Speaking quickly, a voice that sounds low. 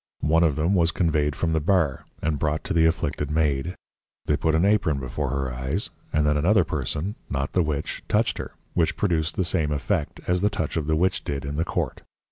Yes: fast, 220 wpm; very low, 80 Hz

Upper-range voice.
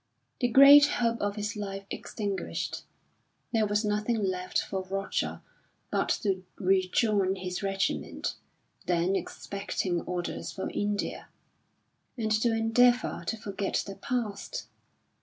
Yes: high, 205 Hz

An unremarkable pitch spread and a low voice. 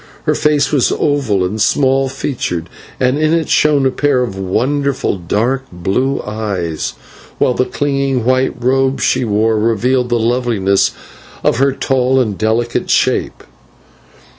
Yes: average, 4.0 semitones; low, 125 Hz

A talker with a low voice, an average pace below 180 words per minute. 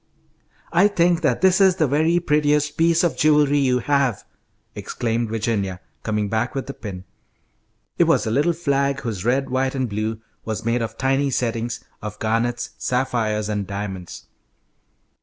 Yes: low, 125 Hz; average, 160 wpm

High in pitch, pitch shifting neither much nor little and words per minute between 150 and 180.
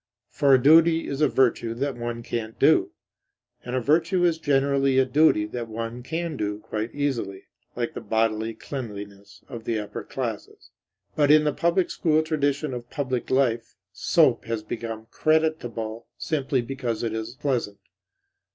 No: low, 125 Hz; average, 4.5 semitones; average, 160 wpm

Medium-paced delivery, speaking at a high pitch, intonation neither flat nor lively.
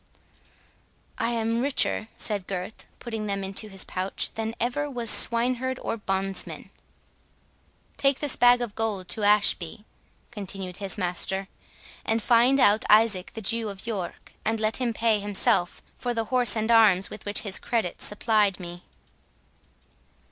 Yes: average, 150 wpm; high, 215 Hz; average, 3.1 semitones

